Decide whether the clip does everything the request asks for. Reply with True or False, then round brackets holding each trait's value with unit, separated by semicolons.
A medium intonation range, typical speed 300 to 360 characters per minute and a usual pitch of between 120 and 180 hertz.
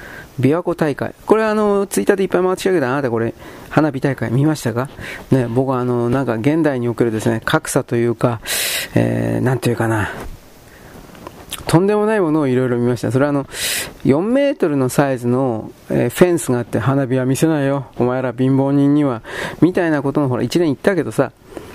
False (4.2 semitones; 400 characters per minute; 135 Hz)